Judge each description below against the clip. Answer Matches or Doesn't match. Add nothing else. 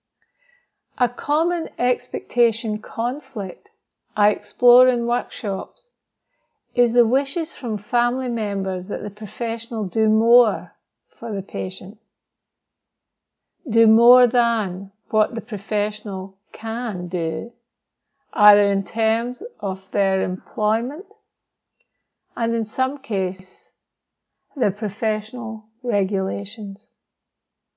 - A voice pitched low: Doesn't match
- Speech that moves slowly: Matches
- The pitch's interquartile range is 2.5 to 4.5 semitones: Matches